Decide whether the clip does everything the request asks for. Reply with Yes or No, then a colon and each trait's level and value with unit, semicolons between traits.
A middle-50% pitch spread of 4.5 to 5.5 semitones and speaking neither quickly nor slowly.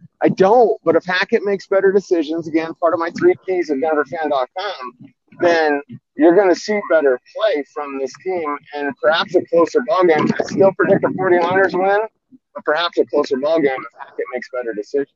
Yes: average, 4.8 semitones; average, 195 wpm